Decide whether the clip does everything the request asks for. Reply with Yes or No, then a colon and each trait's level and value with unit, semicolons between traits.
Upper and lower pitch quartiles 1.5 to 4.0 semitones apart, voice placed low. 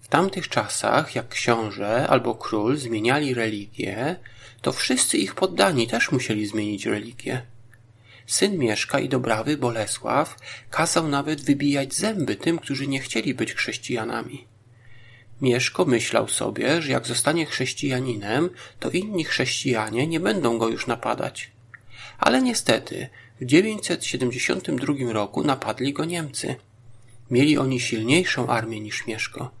Yes: average, 3.5 semitones; low, 120 Hz